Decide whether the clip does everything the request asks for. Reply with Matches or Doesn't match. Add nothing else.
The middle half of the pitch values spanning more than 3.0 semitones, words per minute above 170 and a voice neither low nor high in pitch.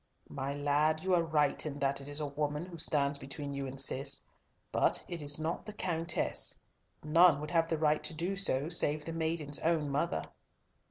Doesn't match